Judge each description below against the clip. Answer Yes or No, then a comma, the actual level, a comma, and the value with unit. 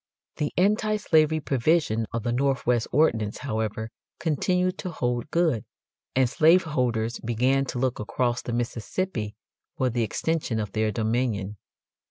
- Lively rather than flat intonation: Yes, wide, 5.8 semitones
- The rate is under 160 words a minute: Yes, average, 140 wpm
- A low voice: Yes, low, 125 Hz